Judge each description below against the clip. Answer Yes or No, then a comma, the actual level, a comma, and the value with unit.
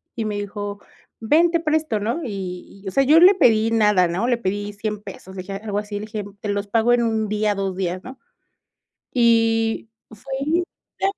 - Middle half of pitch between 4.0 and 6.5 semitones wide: No, average, 2.8 semitones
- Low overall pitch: No, high, 215 Hz